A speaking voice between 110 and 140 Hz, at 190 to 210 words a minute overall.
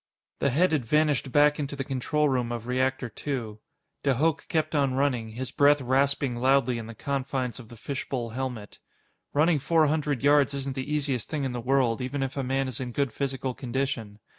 Yes: low, 135 Hz; average, 200 wpm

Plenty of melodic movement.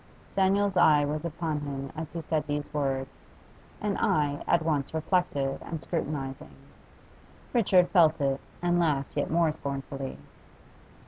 No: average, 3.4 semitones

